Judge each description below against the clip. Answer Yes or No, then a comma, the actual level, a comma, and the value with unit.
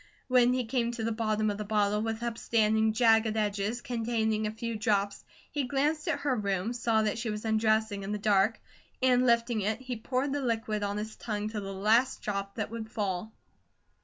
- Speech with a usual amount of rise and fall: No, narrow, 2.1 semitones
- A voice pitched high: Yes, high, 220 Hz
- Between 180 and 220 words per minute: Yes, average, 200 wpm